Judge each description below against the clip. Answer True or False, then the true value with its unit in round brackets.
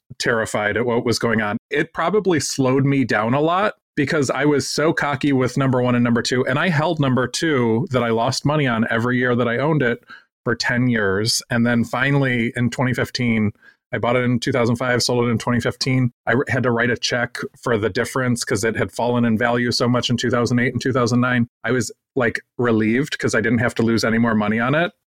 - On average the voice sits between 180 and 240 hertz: False (120 Hz)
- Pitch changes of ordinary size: False (1.8 semitones)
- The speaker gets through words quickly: True (220 wpm)